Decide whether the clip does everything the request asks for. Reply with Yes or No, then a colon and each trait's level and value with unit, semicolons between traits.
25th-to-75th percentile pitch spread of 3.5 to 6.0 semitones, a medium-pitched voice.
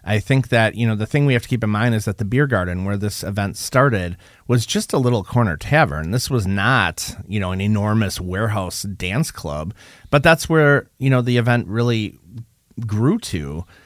No: average, 4.1 semitones; low, 110 Hz